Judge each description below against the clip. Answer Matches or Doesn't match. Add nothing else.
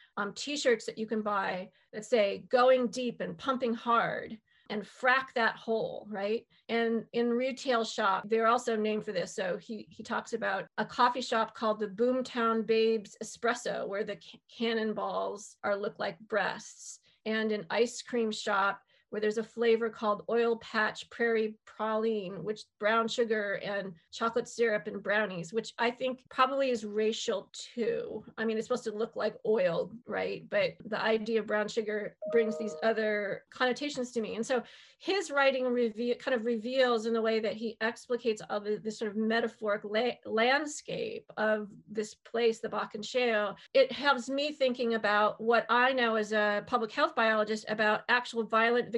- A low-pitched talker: Doesn't match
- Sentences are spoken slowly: Doesn't match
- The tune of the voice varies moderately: Doesn't match